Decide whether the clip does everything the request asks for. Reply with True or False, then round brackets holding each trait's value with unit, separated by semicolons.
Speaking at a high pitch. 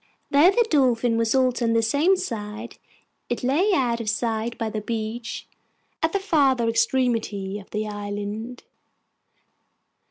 True (235 Hz)